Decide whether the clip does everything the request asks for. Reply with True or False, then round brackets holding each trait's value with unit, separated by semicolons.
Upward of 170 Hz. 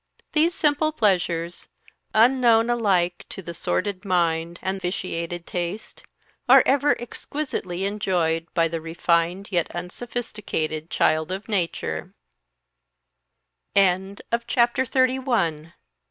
True (185 Hz)